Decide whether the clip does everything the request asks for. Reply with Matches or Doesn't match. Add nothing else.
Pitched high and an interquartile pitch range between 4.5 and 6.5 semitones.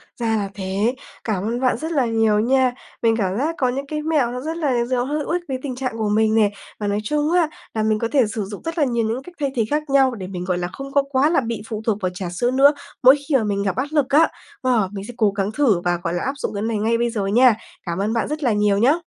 Matches